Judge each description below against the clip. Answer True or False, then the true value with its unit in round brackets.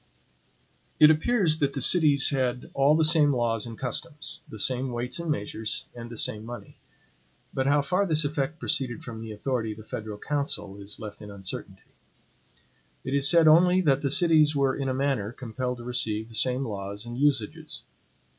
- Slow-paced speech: False (185 wpm)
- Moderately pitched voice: False (130 Hz)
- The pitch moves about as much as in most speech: True (4.7 semitones)